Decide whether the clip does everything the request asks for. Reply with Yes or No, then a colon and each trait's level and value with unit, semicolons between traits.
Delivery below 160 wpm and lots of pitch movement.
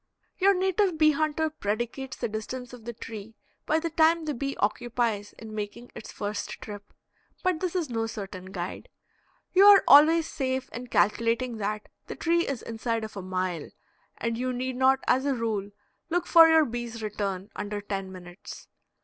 No: average, 175 wpm; wide, 6.6 semitones